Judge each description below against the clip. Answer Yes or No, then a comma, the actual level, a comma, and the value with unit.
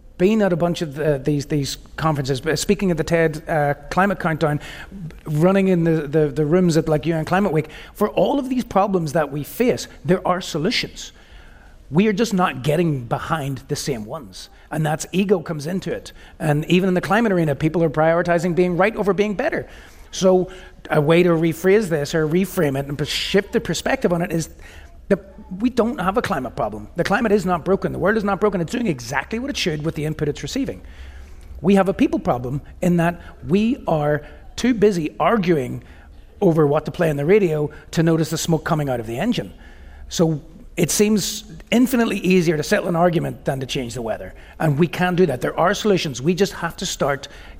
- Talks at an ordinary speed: No, fast, 210 wpm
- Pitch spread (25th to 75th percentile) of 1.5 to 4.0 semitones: No, average, 4.4 semitones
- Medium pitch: Yes, medium, 170 Hz